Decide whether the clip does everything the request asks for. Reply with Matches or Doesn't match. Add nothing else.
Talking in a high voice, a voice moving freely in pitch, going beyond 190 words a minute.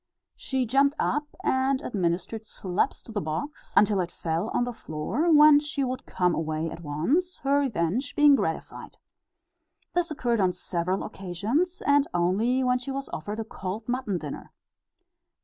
Doesn't match